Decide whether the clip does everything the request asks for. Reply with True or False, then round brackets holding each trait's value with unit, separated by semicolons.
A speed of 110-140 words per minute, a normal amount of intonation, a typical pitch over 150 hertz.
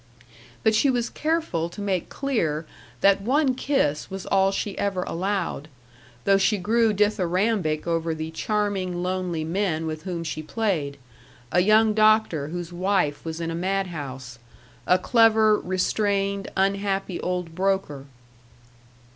True (135 wpm; 4.0 semitones; 190 Hz)